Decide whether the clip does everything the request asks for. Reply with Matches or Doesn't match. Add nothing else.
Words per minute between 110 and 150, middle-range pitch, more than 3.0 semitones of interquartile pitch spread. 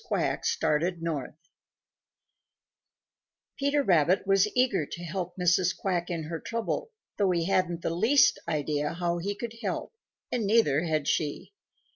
Matches